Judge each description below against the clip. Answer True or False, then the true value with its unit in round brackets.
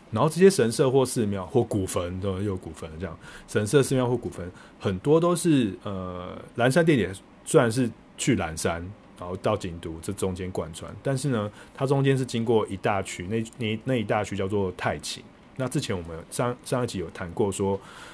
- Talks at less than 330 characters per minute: True (280 characters per minute)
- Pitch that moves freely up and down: True (5.7 semitones)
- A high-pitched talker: False (105 Hz)